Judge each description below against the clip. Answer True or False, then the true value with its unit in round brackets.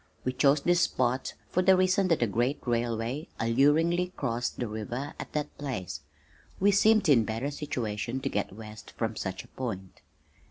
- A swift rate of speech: False (170 wpm)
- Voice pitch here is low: True (130 Hz)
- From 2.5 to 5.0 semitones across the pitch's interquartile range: False (5.4 semitones)